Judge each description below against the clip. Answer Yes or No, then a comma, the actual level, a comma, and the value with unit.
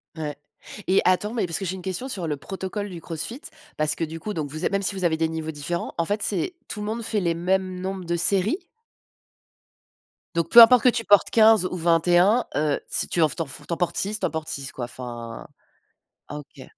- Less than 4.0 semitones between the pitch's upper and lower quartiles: No, average, 4.3 semitones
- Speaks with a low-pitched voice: No, medium, 180 Hz